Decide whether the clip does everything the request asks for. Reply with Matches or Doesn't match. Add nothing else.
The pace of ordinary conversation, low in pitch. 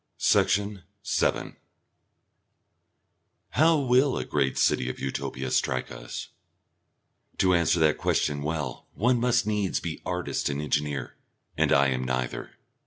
Doesn't match